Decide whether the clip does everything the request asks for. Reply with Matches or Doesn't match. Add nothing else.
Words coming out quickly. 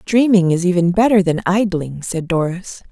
Doesn't match